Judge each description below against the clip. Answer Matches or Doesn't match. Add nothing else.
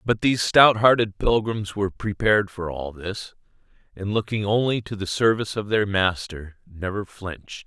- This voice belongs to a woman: Doesn't match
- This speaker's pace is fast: Doesn't match